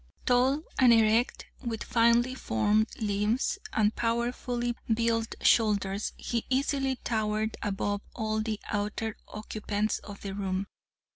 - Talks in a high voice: Yes, high, 220 Hz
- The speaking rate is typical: No, slow, 125 wpm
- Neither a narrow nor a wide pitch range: No, narrow, 2.3 semitones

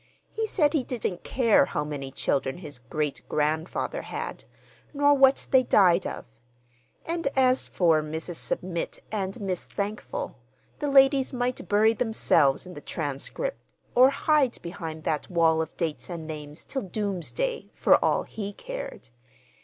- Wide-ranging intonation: Yes, wide, 8.9 semitones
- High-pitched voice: Yes, high, 195 Hz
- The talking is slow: No, average, 145 wpm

